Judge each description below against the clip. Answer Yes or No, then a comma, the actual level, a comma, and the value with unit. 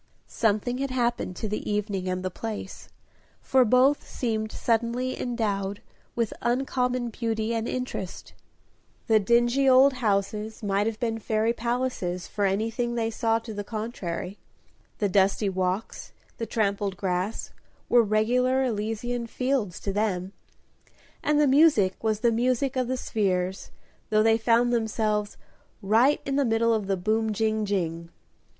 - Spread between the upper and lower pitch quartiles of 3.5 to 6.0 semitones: No, average, 3.0 semitones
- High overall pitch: Yes, high, 225 Hz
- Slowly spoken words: No, average, 145 wpm